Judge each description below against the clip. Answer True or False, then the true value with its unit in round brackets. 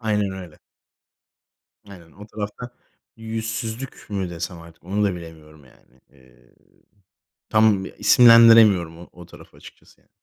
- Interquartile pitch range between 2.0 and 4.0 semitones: False (4.8 semitones)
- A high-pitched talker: False (95 Hz)